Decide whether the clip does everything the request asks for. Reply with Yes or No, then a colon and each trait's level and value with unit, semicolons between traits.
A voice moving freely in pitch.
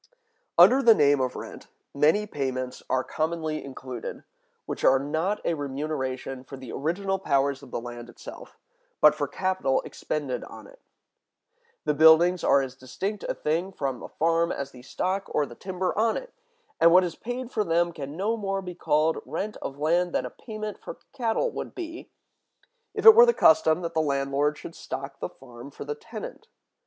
Yes: wide, 5.9 semitones